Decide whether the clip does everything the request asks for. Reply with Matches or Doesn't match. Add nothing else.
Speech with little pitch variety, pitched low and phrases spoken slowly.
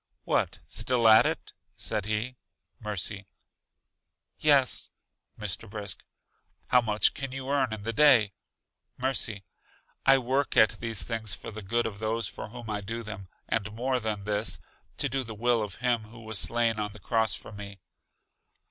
Doesn't match